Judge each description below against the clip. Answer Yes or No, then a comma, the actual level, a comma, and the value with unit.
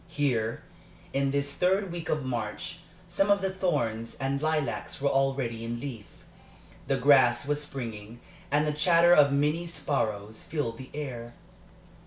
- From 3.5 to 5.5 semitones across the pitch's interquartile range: Yes, average, 4.4 semitones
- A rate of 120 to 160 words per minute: Yes, average, 150 wpm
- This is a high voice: No, medium, 140 Hz